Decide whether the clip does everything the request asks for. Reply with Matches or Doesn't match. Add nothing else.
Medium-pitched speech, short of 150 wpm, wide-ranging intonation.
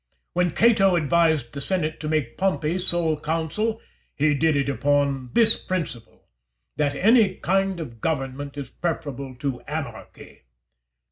Doesn't match